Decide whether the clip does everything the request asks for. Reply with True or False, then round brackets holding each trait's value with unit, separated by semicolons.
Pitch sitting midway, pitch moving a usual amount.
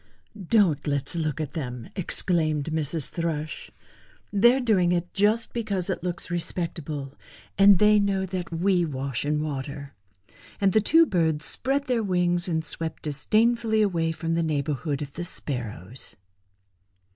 True (170 Hz; 4.8 semitones)